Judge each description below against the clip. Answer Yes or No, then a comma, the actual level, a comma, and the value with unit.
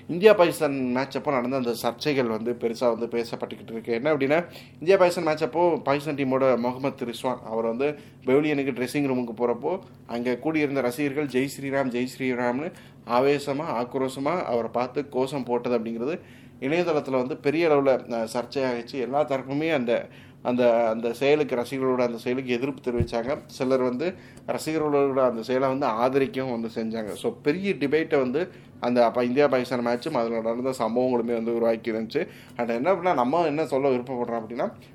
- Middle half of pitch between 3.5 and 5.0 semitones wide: No, average, 2.9 semitones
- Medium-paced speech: No, fast, 155 wpm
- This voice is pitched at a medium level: No, low, 130 Hz